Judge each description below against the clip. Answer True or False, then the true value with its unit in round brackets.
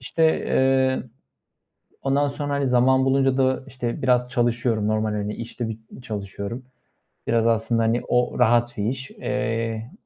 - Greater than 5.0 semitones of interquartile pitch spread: False (2.6 semitones)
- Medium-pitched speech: False (120 Hz)